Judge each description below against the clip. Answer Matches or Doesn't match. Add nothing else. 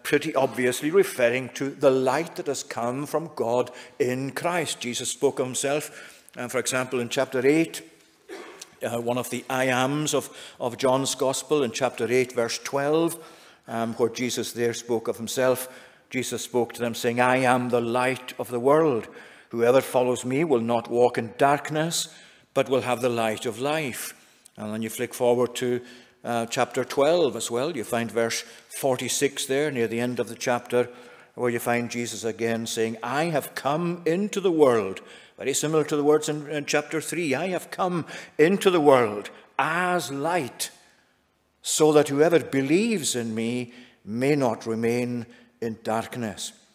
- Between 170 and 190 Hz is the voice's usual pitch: Doesn't match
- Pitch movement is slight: Doesn't match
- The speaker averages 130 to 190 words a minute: Matches